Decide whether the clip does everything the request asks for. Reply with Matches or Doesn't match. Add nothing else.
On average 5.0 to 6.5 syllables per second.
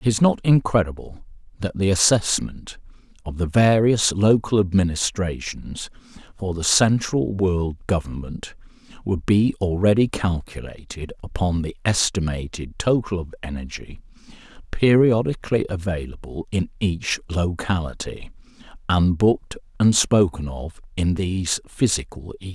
Doesn't match